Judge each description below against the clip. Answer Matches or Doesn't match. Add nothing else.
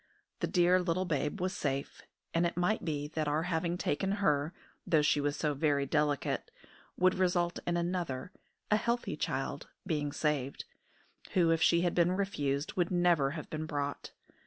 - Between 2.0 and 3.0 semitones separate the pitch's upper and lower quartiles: Doesn't match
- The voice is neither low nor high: Matches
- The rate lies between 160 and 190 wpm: Matches